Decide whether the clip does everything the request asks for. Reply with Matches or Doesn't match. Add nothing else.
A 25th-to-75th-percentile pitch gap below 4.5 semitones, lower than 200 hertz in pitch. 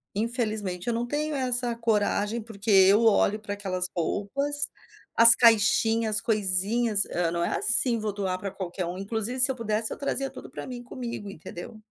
Doesn't match